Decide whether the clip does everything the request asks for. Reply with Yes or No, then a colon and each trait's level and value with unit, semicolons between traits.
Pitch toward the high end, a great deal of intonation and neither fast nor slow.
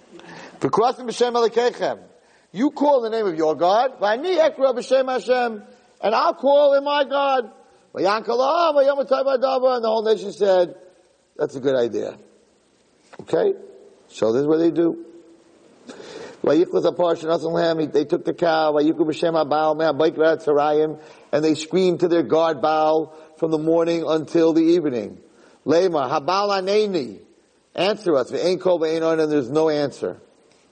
No: medium, 180 Hz; wide, 8.4 semitones; average, 170 wpm